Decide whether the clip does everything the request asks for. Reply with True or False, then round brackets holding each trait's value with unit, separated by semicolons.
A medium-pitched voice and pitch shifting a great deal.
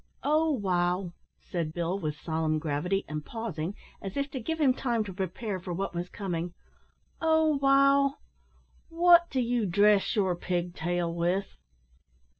False (195 Hz; 7.3 semitones)